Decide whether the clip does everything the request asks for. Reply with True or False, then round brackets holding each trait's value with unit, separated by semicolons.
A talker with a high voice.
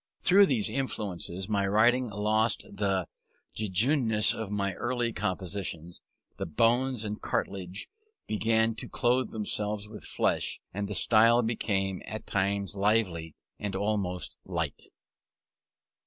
False (105 Hz)